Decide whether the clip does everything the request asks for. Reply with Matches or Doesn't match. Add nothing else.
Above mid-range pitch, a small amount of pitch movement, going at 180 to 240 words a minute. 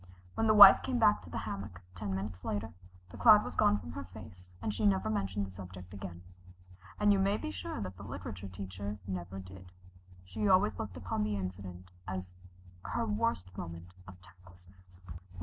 Doesn't match